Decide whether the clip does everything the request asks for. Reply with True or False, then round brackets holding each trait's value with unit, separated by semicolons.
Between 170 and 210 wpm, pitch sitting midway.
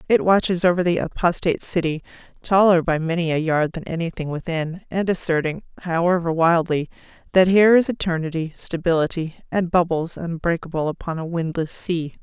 False (145 wpm; 170 Hz)